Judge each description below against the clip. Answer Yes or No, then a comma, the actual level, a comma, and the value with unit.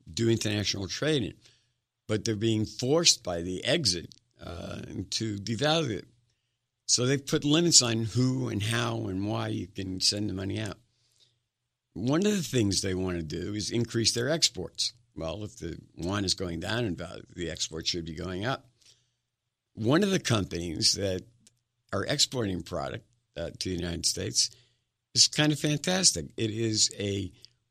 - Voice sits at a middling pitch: No, low, 115 Hz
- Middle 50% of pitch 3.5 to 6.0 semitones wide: Yes, average, 3.8 semitones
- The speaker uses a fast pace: No, average, 165 wpm